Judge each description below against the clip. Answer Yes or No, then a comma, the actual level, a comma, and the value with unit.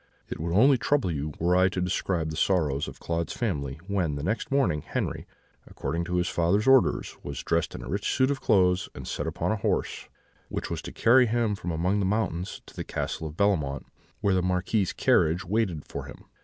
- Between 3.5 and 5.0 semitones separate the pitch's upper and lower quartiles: Yes, average, 4.1 semitones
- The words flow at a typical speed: No, fast, 210 wpm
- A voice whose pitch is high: No, very low, 90 Hz